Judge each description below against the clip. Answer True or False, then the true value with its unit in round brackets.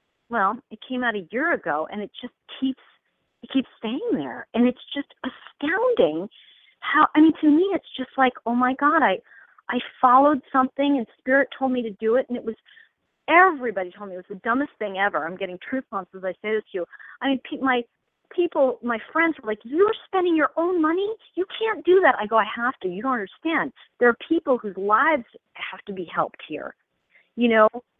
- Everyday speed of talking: False (215 wpm)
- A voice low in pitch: False (255 Hz)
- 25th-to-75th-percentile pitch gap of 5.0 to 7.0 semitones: True (5.6 semitones)